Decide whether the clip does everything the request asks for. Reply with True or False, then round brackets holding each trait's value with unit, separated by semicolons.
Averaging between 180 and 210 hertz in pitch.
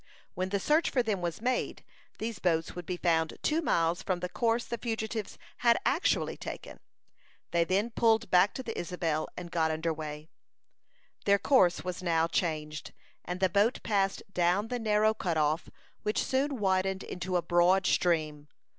True (185 Hz)